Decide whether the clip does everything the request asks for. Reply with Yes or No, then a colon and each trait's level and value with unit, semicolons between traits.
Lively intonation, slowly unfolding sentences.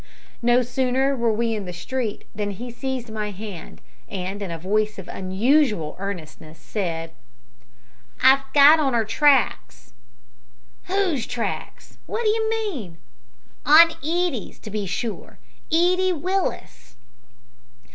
Yes: wide, 6.7 semitones; slow, 125 wpm